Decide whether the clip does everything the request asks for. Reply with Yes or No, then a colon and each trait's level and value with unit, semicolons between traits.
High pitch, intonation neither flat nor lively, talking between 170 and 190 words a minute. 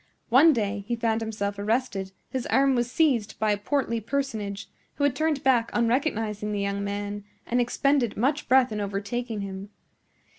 Yes: high, 230 Hz; average, 4.2 semitones; average, 175 wpm